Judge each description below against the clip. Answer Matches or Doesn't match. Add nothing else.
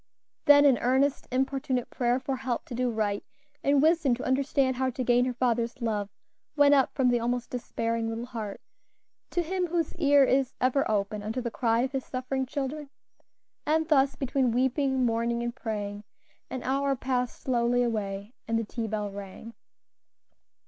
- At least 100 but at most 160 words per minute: Doesn't match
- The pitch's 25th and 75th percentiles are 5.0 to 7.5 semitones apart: Doesn't match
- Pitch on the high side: Matches